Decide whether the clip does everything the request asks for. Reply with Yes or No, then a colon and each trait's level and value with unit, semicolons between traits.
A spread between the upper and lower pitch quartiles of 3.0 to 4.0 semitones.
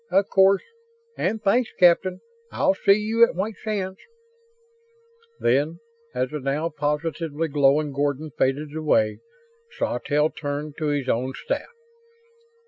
No: average, 4.9 semitones